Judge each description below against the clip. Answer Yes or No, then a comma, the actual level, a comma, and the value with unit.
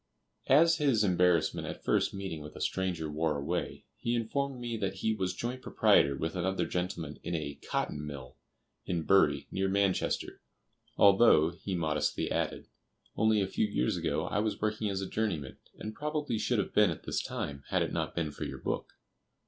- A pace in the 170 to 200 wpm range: Yes, average, 185 wpm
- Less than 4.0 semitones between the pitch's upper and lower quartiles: No, average, 5.3 semitones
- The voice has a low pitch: Yes, very low, 95 Hz